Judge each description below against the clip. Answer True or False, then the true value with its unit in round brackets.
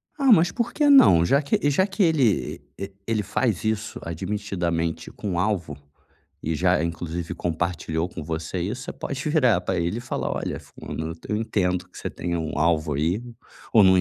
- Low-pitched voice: True (95 Hz)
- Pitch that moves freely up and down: True (6.4 semitones)